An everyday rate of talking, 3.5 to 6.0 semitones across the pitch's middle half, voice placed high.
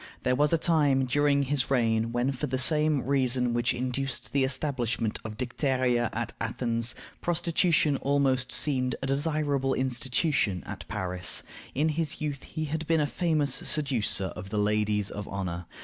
No: average, 160 wpm; average, 3.9 semitones; low, 130 Hz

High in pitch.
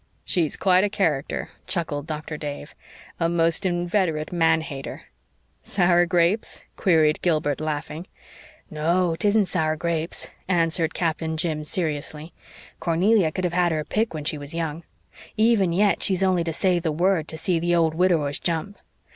No: medium, 165 Hz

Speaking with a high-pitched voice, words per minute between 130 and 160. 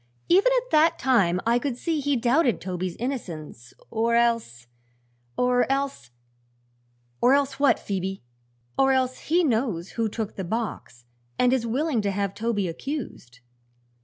Yes: high, 235 Hz; average, 150 wpm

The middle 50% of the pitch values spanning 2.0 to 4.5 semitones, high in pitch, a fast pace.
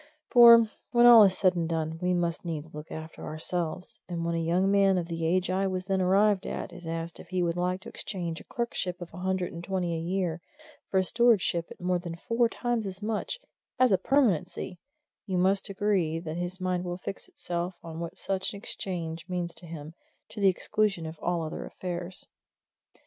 No: narrow, 2.4 semitones; medium, 180 Hz; fast, 210 wpm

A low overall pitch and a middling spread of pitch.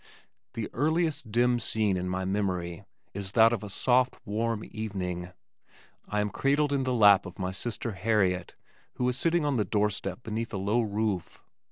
Yes: low, 105 Hz; average, 4.0 semitones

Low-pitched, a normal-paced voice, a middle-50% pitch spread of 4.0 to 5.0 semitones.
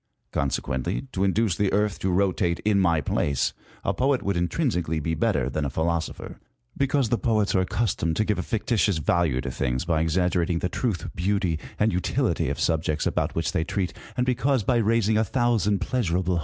Yes: very low, 95 Hz; average, 185 wpm; average, 4.7 semitones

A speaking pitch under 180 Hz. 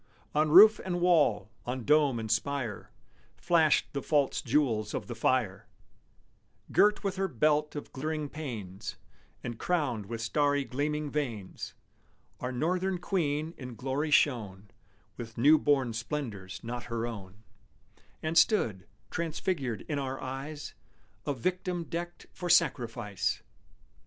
Yes: medium, 140 Hz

